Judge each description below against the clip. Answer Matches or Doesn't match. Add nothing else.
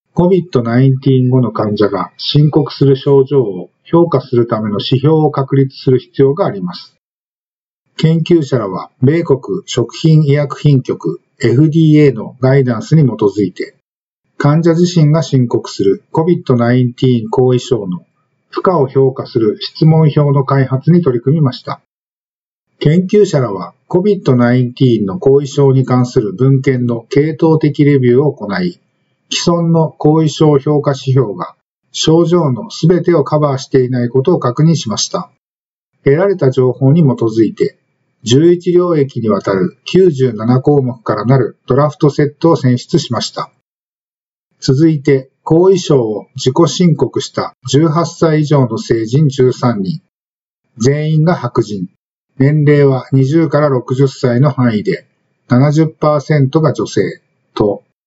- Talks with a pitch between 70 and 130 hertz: Doesn't match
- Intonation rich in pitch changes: Doesn't match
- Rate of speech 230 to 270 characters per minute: Matches